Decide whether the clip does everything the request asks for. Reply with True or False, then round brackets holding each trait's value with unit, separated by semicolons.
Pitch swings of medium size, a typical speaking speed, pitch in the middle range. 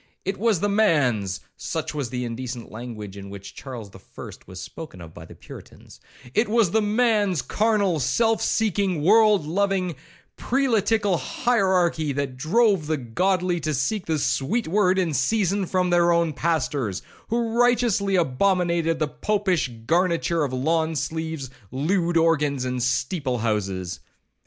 False (7.4 semitones; 145 wpm; 165 Hz)